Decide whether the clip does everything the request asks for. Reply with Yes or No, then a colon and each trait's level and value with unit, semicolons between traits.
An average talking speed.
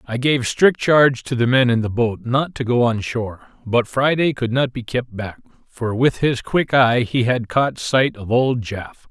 No: fast, 235 wpm